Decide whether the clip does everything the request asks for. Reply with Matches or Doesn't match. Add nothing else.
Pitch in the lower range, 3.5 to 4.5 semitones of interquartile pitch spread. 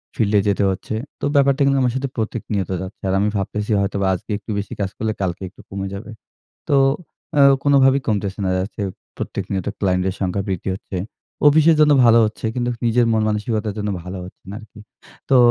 Matches